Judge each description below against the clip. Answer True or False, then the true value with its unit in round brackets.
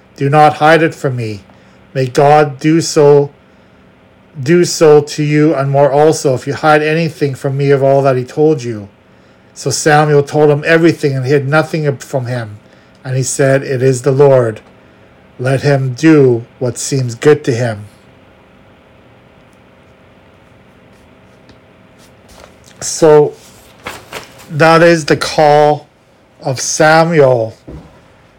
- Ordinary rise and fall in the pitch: True (3.5 semitones)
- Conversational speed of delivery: False (130 wpm)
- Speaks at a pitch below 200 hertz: True (140 Hz)